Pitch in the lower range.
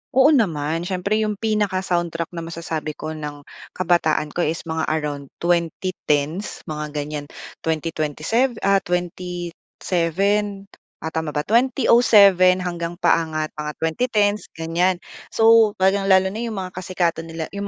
No: medium, 175 Hz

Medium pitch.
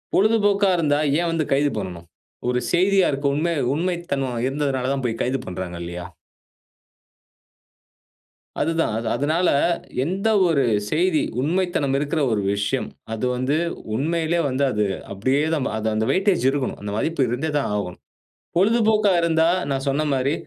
Yes: medium, 145 Hz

